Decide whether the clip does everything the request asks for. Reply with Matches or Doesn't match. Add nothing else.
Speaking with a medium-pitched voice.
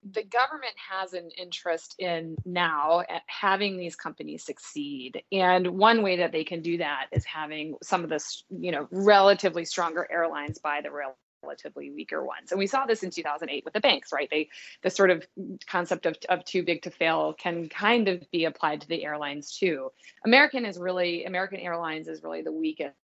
Matches